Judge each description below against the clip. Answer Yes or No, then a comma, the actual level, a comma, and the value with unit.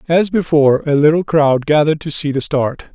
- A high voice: No, medium, 150 Hz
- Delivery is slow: No, fast, 205 wpm